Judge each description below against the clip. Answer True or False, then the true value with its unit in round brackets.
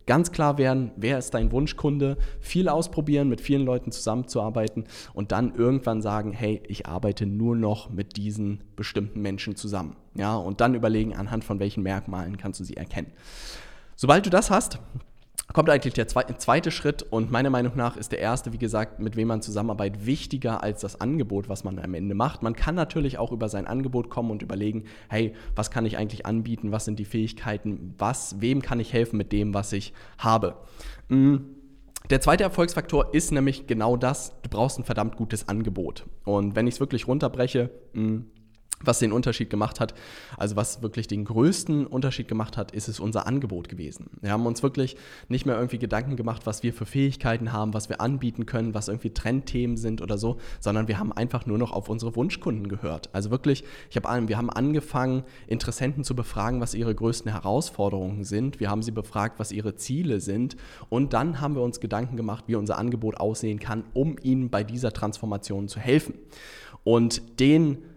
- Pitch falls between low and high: False (115 Hz)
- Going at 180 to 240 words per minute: True (190 wpm)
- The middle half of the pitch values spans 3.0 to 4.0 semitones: True (3.4 semitones)